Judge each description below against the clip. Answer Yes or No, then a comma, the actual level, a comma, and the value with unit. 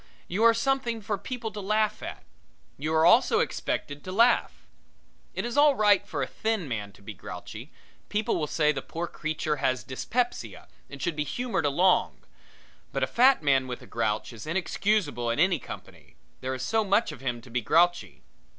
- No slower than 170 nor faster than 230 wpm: Yes, average, 190 wpm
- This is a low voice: No, medium, 175 Hz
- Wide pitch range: Yes, wide, 8.3 semitones